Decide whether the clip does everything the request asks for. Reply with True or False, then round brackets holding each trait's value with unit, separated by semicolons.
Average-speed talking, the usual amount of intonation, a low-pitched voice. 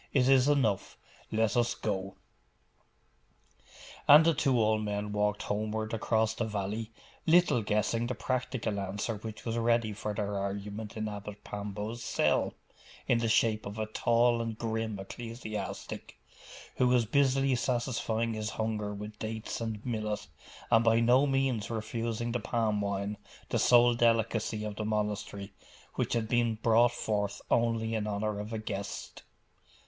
False (150 wpm; 2.1 semitones; 110 Hz)